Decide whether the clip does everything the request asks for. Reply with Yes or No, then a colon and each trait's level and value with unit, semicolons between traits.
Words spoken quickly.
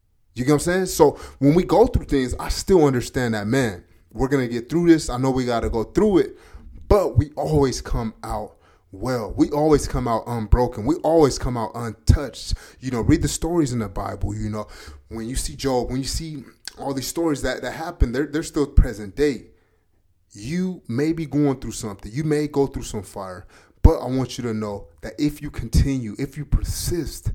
Yes: fast, 215 wpm